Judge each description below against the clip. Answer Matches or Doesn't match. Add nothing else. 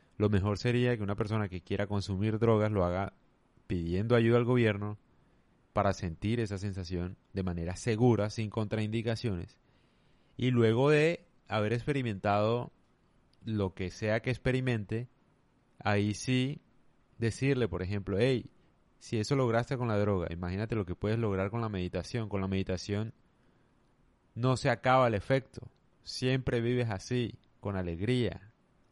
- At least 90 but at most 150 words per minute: Matches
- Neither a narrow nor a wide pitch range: Matches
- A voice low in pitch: Matches